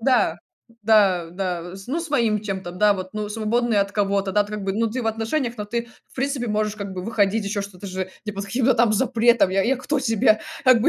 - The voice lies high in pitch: Yes, high, 210 Hz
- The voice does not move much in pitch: No, average, 3.1 semitones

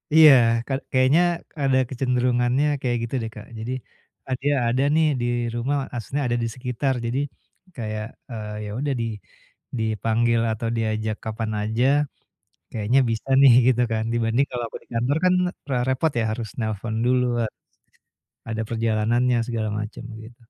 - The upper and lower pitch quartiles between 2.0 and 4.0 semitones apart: Yes, average, 2.7 semitones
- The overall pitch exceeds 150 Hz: No, low, 120 Hz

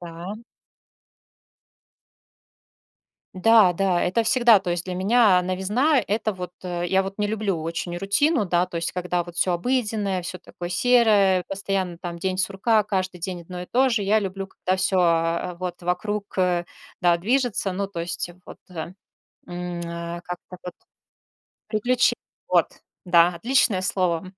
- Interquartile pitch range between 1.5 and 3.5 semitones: Yes, average, 2.9 semitones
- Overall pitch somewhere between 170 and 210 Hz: Yes, medium, 185 Hz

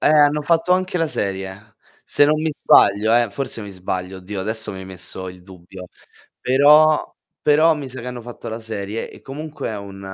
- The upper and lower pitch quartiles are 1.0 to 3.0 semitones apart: No, wide, 7.4 semitones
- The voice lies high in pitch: No, low, 110 Hz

